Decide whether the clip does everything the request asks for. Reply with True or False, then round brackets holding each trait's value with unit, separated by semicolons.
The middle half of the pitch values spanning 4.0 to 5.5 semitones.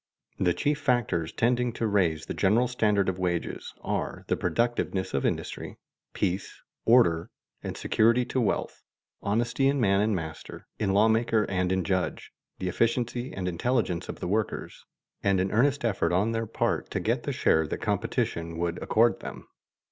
True (4.5 semitones)